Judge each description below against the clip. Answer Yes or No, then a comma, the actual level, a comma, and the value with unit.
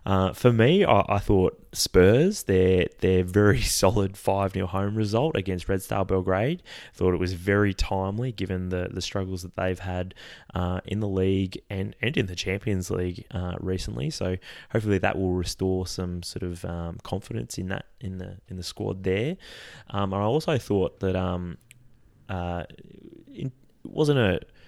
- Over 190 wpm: No, average, 175 wpm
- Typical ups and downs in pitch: No, narrow, 2.3 semitones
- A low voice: Yes, very low, 95 Hz